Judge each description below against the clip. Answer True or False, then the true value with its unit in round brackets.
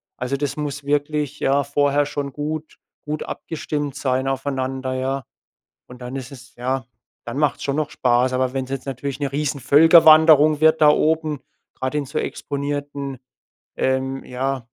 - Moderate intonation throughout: False (2.0 semitones)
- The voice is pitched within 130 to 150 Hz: True (140 Hz)